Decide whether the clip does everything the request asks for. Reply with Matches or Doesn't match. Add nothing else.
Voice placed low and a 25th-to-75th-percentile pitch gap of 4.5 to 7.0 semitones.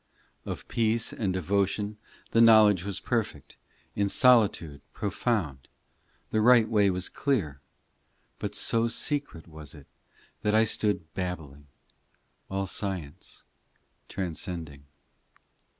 Matches